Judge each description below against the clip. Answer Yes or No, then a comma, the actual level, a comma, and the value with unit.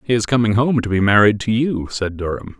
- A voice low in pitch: Yes, low, 110 Hz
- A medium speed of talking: No, fast, 255 wpm